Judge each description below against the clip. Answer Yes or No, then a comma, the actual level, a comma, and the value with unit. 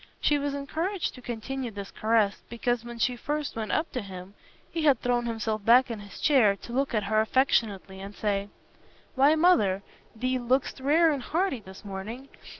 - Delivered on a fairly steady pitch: No, average, 4.8 semitones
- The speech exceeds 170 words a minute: Yes, average, 185 wpm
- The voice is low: No, high, 240 Hz